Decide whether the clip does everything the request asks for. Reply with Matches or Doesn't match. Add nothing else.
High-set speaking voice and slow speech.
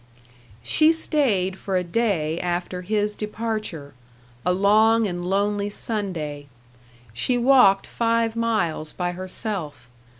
Matches